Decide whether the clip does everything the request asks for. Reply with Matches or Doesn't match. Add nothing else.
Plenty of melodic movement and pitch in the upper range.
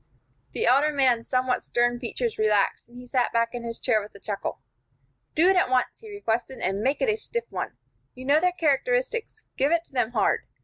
Matches